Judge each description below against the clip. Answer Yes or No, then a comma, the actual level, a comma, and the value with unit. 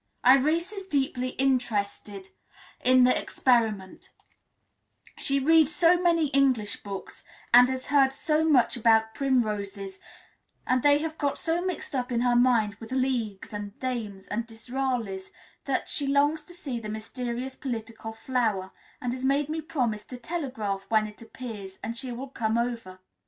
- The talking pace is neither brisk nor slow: Yes, average, 155 wpm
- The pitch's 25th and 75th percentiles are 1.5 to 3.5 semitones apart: No, average, 4.0 semitones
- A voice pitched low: No, very high, 250 Hz